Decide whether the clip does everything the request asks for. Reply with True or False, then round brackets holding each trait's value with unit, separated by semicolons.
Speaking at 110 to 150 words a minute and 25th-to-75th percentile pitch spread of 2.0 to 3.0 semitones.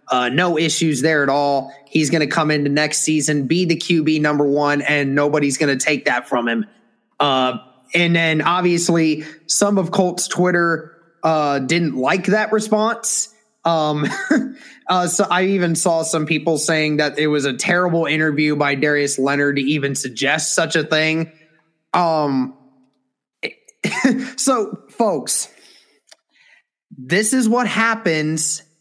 False (140 wpm; 3.5 semitones)